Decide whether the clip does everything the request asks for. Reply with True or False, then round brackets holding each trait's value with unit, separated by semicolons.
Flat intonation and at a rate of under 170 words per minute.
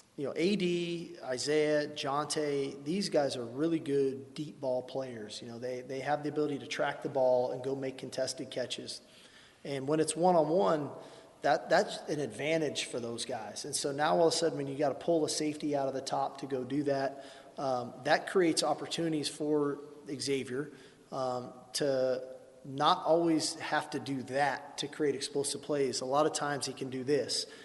False (2.3 semitones; 195 wpm)